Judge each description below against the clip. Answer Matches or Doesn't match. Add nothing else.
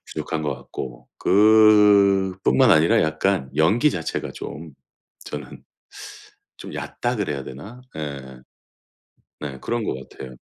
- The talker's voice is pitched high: Doesn't match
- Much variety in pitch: Matches